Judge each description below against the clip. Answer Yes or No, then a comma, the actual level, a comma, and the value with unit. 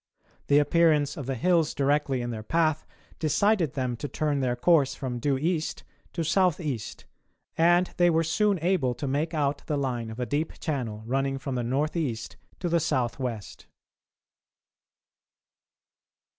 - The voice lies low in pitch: No, medium, 145 Hz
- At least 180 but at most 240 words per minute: No, average, 160 wpm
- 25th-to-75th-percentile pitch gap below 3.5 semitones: No, average, 4.3 semitones